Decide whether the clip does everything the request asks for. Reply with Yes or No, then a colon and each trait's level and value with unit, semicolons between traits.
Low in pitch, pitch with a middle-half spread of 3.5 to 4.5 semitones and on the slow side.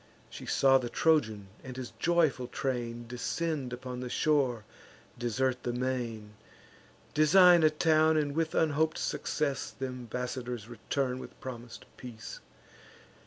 Yes: low, 130 Hz; average, 4.0 semitones; slow, 125 wpm